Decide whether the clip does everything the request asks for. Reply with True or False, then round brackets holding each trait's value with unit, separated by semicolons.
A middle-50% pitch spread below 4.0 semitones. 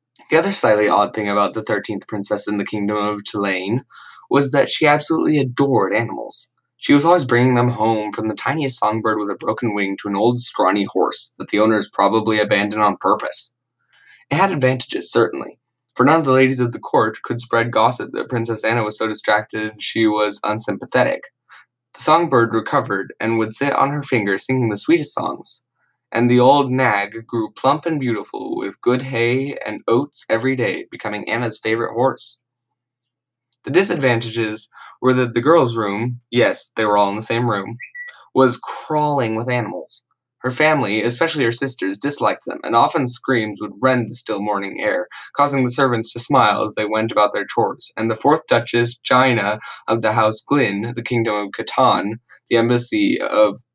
True (3.2 semitones)